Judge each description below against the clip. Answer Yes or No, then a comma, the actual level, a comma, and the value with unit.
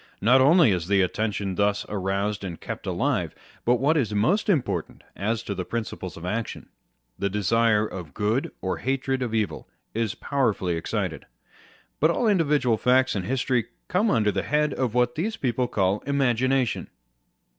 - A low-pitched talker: Yes, low, 115 Hz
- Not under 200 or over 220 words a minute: No, average, 165 wpm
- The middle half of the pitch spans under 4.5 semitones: No, average, 4.8 semitones